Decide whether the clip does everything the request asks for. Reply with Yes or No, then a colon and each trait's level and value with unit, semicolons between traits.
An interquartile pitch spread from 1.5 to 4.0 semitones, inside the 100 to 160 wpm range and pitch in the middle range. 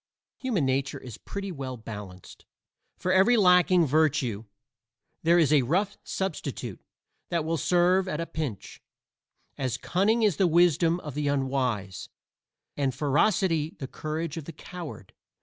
No: average, 5.3 semitones; average, 140 wpm; medium, 155 Hz